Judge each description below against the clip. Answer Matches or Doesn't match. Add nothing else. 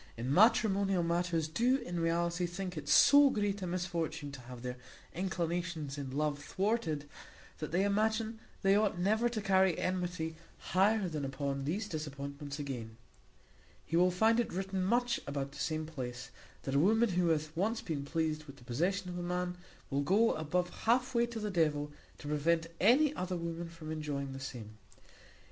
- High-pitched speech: Doesn't match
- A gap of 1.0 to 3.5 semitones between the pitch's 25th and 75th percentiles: Doesn't match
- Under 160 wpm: Doesn't match